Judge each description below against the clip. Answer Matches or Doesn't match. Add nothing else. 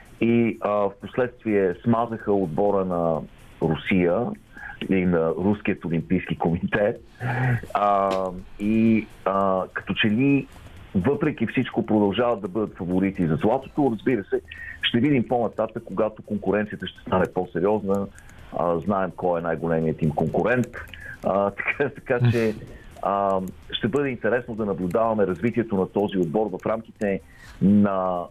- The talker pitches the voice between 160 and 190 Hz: Doesn't match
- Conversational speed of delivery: Matches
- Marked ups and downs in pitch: Doesn't match